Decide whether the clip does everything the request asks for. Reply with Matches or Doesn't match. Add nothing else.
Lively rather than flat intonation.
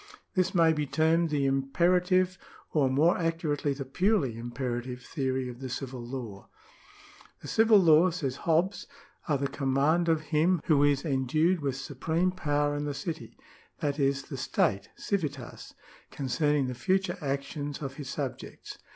Doesn't match